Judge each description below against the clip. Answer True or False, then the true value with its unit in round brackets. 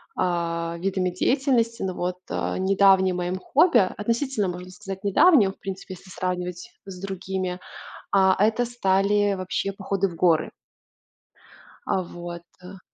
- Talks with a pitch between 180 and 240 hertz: True (190 Hz)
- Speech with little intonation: True (1.9 semitones)